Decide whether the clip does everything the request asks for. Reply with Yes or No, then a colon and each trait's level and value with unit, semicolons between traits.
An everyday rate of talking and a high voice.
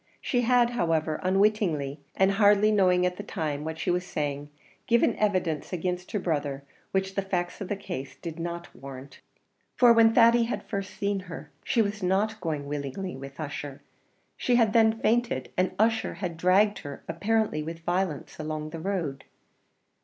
No: average, 170 wpm; medium, 180 Hz